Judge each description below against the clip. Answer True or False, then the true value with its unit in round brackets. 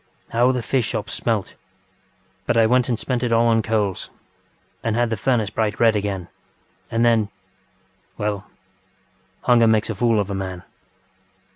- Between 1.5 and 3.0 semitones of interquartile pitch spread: True (2.6 semitones)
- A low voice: True (110 Hz)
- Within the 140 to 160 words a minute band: True (155 wpm)